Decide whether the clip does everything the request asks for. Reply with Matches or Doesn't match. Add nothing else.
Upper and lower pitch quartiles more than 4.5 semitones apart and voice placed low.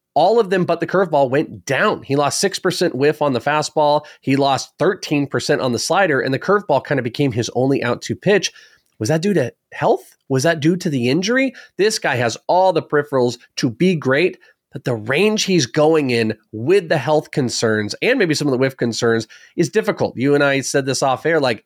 Doesn't match